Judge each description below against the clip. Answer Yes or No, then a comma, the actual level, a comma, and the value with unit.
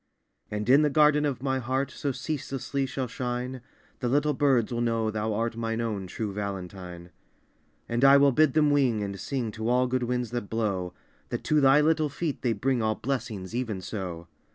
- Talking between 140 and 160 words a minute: No, average, 195 wpm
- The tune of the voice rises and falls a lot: No, average, 4.1 semitones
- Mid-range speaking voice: No, low, 120 Hz